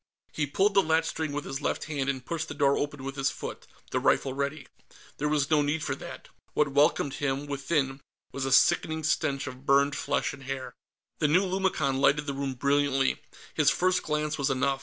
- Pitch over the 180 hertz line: No, medium, 145 Hz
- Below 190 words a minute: No, average, 200 wpm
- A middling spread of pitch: No, narrow, 2.0 semitones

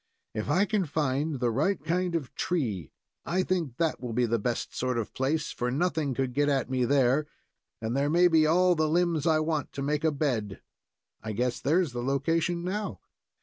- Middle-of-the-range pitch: Yes, medium, 145 Hz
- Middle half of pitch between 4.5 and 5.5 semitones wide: Yes, average, 4.9 semitones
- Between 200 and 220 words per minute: Yes, fast, 205 wpm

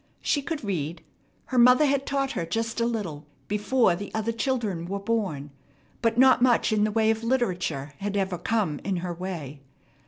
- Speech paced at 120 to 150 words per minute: No, average, 185 wpm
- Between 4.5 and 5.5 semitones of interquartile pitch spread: Yes, average, 5.2 semitones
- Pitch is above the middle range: Yes, high, 210 Hz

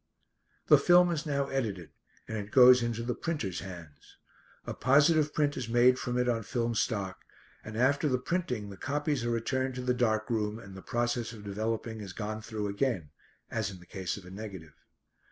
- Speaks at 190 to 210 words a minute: Yes, average, 195 wpm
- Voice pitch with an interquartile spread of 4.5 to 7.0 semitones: No, average, 4.0 semitones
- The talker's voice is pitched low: Yes, low, 115 Hz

